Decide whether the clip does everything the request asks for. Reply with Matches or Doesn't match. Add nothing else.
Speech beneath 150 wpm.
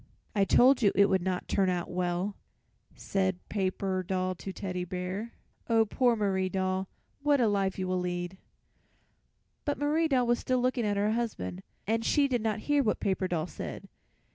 Doesn't match